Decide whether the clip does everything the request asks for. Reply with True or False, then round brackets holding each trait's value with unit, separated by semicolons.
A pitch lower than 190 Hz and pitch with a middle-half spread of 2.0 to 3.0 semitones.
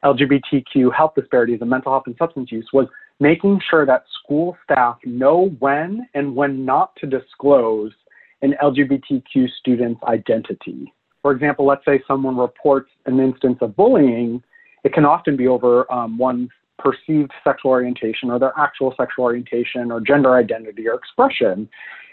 True (135 Hz; 2.6 semitones)